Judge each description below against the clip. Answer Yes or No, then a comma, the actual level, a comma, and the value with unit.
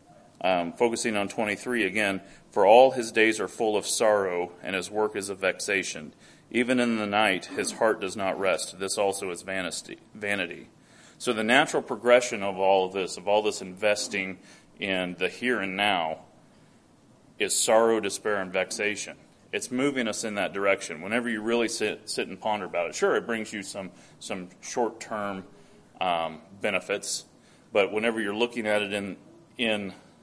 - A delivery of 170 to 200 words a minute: Yes, average, 175 wpm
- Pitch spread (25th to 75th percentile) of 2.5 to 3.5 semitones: Yes, average, 3.2 semitones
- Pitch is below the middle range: Yes, low, 105 Hz